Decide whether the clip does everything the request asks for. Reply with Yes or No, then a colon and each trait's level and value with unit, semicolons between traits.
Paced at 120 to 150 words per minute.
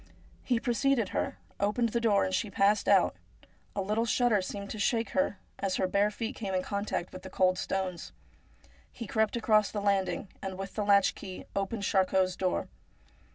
No: average, 185 wpm